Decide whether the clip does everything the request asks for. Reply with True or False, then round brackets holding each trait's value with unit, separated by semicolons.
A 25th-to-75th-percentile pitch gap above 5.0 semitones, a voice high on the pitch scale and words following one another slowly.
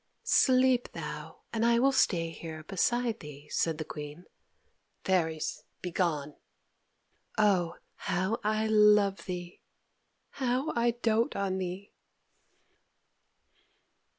True (5.5 semitones; 195 Hz; 100 wpm)